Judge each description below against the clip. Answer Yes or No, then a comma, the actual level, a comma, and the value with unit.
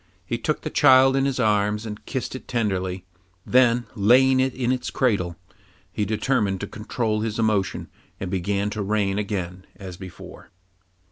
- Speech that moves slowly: No, average, 160 wpm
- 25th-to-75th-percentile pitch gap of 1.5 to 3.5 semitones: No, average, 4.2 semitones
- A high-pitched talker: No, low, 105 Hz